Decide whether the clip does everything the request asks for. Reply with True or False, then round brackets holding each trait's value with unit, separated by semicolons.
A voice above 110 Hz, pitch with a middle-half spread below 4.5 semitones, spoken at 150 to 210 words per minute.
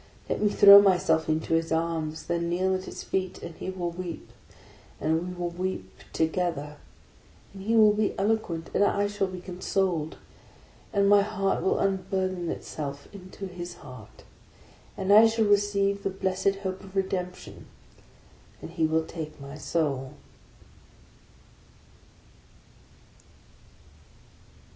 False (185 Hz; 3.3 semitones; 140 wpm)